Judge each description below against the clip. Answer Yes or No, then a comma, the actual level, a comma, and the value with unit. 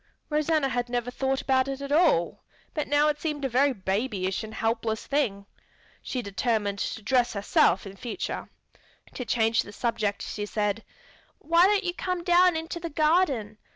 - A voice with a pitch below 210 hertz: No, very high, 255 Hz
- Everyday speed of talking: Yes, average, 170 wpm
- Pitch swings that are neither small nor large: No, wide, 5.9 semitones